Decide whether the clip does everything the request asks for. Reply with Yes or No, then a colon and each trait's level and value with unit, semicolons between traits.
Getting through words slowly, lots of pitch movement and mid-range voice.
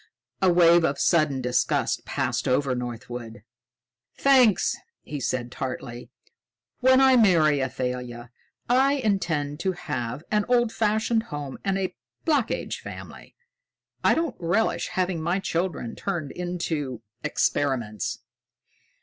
Yes: slow, 120 wpm; wide, 8.3 semitones; medium, 165 Hz